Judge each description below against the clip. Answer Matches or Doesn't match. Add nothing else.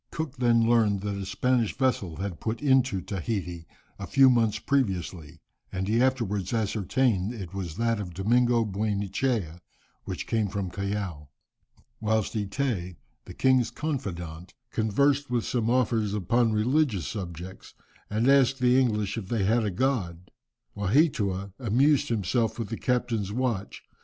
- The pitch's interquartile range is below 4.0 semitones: Doesn't match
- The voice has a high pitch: Doesn't match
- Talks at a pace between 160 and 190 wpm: Doesn't match